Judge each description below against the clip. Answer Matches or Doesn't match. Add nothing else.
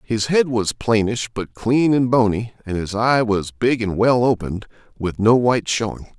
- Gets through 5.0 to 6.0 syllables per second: Doesn't match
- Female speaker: Doesn't match